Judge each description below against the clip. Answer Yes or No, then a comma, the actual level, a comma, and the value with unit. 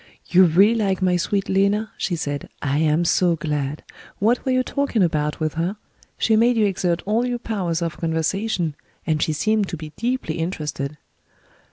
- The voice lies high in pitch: No, medium, 180 Hz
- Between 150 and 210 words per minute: Yes, average, 180 wpm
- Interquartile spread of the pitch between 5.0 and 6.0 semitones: Yes, wide, 5.4 semitones